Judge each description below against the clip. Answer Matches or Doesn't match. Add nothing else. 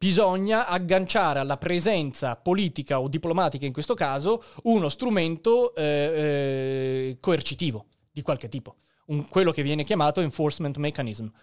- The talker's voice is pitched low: Doesn't match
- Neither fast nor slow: Matches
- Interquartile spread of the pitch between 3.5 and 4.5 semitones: Doesn't match